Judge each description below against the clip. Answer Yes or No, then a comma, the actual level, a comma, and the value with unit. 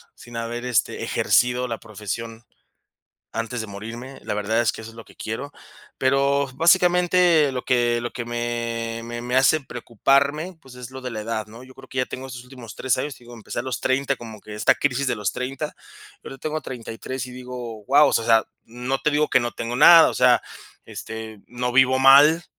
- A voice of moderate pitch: No, low, 125 Hz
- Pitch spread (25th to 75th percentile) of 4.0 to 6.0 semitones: No, average, 2.7 semitones